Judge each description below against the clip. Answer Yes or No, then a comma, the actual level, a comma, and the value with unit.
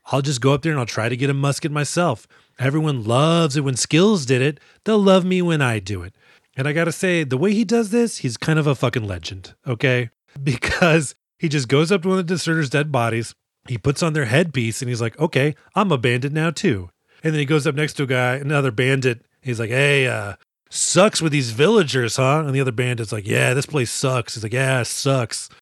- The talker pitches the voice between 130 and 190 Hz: Yes, medium, 140 Hz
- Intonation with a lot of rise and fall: No, average, 4.4 semitones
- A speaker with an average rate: No, fast, 240 wpm